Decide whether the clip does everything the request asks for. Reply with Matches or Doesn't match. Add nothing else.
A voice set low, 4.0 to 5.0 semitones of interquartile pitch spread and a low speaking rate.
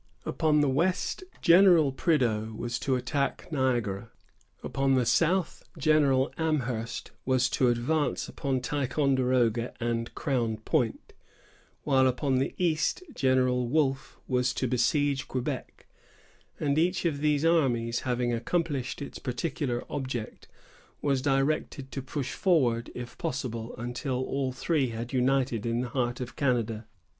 Doesn't match